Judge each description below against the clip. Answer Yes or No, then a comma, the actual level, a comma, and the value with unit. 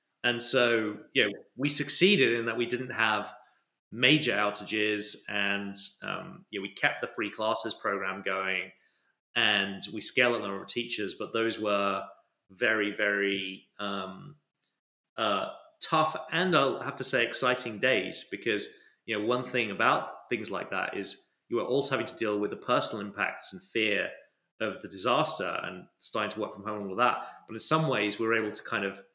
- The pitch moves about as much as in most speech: Yes, average, 3.6 semitones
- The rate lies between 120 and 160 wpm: No, average, 185 wpm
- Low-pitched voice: Yes, low, 110 Hz